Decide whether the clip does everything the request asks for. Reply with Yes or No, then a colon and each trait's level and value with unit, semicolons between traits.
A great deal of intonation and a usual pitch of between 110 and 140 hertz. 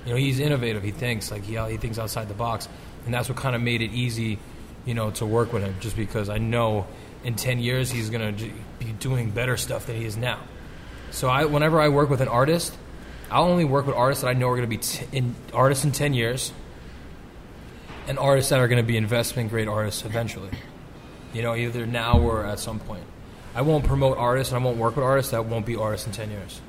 No: average, 2.7 semitones; low, 115 Hz